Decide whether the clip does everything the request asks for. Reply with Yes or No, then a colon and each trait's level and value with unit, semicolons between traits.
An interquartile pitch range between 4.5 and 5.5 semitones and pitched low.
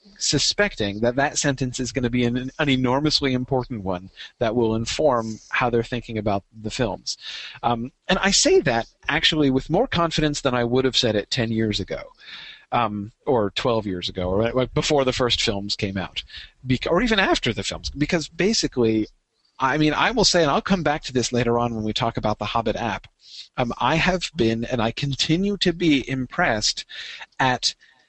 Yes: average, 5.1 semitones; low, 125 Hz